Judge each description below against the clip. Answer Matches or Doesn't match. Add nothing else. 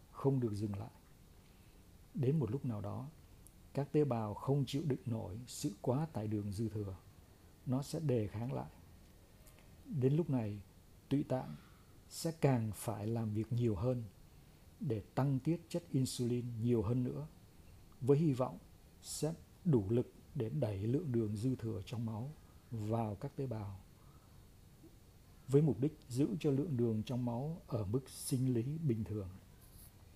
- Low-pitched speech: Matches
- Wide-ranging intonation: Doesn't match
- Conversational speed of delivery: Doesn't match